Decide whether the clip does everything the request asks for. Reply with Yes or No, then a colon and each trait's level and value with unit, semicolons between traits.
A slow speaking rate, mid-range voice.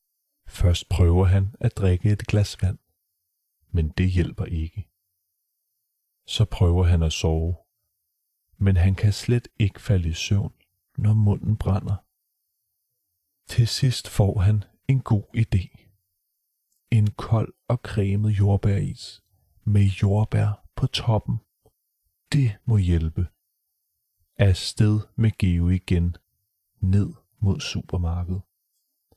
No: slow, 110 wpm; low, 100 Hz